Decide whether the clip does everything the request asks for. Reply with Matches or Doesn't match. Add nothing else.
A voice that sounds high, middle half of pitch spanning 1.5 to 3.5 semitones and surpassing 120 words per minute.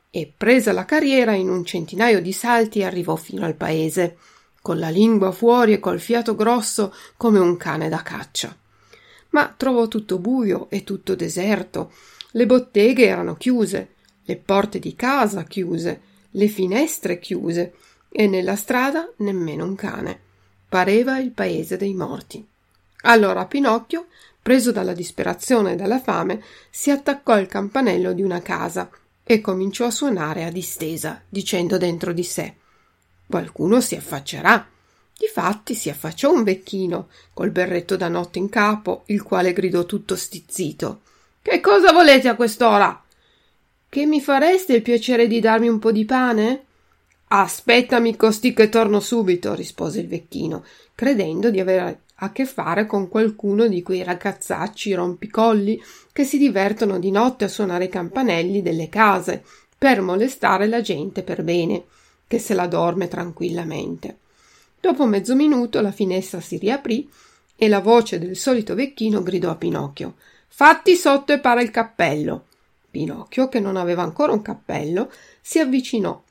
Doesn't match